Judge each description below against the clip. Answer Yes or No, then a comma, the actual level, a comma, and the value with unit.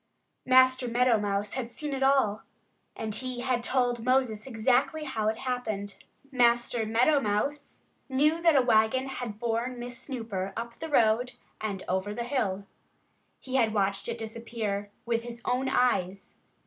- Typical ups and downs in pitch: Yes, average, 3.0 semitones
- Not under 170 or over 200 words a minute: No, average, 155 wpm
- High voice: Yes, high, 240 Hz